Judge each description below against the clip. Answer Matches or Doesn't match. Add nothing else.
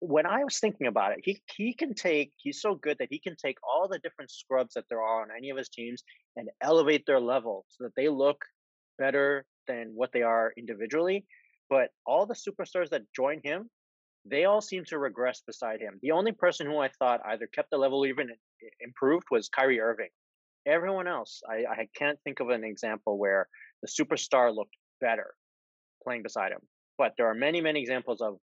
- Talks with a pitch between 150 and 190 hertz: Doesn't match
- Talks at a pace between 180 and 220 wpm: Matches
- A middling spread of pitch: Doesn't match